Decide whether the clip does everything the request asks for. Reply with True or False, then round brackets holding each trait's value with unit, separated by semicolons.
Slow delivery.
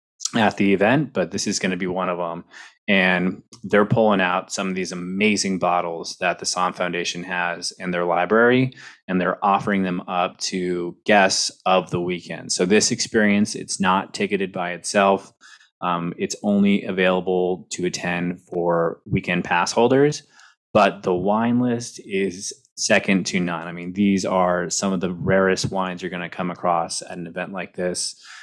False (175 wpm)